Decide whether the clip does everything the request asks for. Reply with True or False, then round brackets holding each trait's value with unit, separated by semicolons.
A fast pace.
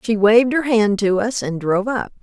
True (245 wpm)